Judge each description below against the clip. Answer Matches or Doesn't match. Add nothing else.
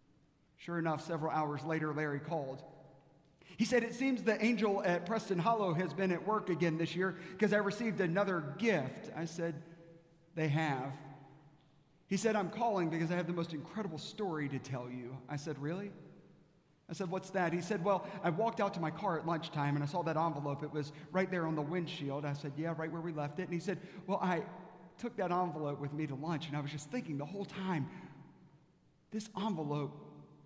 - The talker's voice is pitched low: Doesn't match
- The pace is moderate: Doesn't match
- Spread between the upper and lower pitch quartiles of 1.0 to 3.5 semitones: Doesn't match